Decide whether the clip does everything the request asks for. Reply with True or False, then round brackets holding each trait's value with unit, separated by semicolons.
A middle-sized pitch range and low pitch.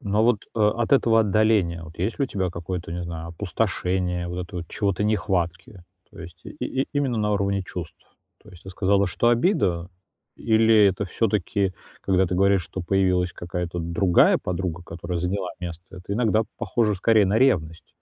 True (3.3 semitones; 95 Hz)